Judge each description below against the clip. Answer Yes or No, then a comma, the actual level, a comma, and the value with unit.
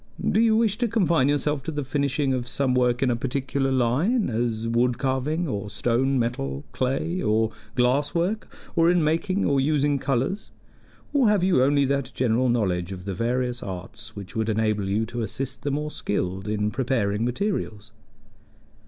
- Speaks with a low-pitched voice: Yes, low, 130 Hz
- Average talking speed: Yes, average, 175 wpm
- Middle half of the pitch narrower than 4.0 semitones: No, average, 4.7 semitones